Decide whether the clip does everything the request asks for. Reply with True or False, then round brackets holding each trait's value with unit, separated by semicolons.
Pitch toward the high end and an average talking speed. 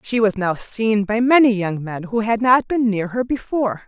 False (220 Hz; 230 wpm)